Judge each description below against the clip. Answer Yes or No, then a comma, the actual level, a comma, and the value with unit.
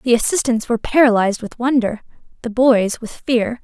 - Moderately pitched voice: No, high, 235 Hz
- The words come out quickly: No, average, 165 wpm